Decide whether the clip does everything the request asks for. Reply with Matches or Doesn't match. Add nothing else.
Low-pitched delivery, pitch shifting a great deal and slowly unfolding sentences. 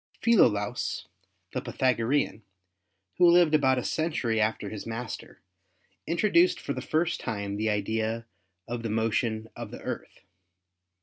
Matches